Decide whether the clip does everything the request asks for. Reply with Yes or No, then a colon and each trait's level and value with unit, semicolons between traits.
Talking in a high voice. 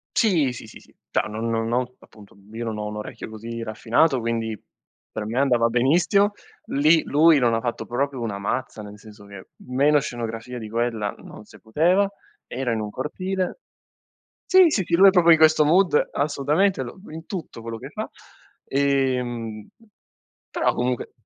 No: low, 125 Hz